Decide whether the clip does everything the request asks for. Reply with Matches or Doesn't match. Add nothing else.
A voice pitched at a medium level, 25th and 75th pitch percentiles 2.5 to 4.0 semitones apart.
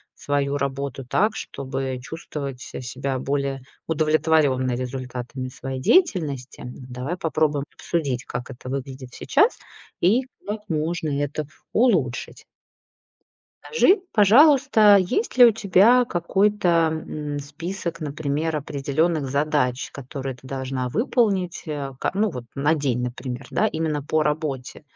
Doesn't match